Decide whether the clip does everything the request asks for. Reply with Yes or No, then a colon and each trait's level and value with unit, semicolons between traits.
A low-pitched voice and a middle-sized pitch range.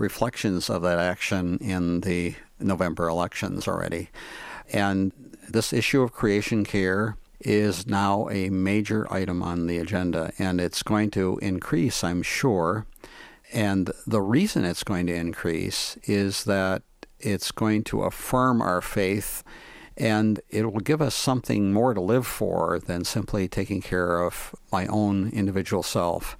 Yes: low, 100 Hz; average, 3.0 semitones